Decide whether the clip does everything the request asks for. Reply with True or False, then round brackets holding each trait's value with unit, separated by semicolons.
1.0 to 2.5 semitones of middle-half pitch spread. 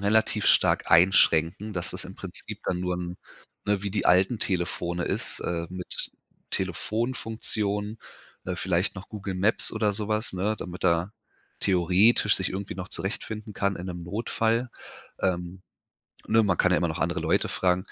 False (2.9 semitones)